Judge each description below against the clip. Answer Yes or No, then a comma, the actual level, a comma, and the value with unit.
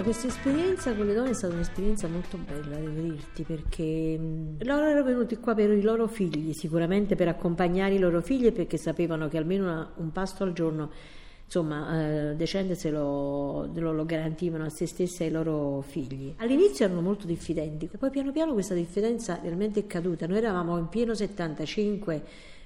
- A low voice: No, medium, 175 Hz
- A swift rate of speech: Yes, fast, 175 wpm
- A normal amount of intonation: Yes, average, 4.5 semitones